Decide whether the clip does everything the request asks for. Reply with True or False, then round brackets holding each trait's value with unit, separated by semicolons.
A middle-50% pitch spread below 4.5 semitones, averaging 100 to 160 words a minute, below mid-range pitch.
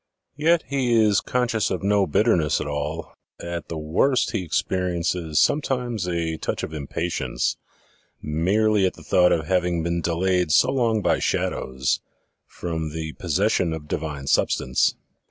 False (5.1 semitones; 155 wpm; 90 Hz)